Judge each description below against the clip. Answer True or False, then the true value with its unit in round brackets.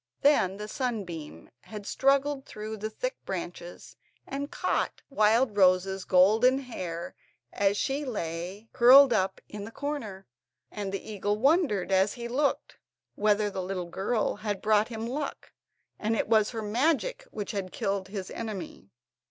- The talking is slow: False (145 wpm)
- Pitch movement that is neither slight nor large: True (4.7 semitones)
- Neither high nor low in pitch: False (210 Hz)